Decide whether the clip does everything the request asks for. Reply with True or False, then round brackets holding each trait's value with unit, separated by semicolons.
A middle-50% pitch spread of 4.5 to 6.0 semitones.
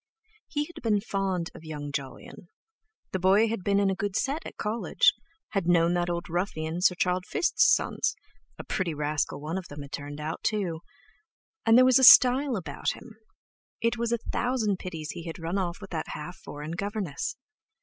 True (4.8 semitones)